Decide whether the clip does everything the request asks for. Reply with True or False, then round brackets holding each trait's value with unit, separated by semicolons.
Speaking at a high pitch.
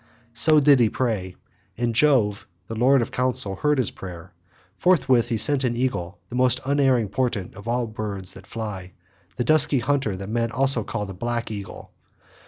False (120 Hz)